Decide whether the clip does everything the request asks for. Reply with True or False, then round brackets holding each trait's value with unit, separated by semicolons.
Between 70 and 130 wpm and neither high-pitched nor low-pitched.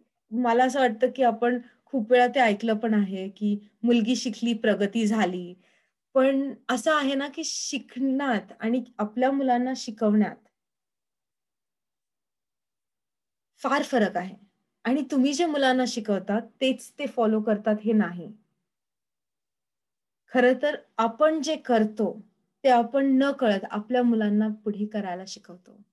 False (125 wpm; 235 Hz)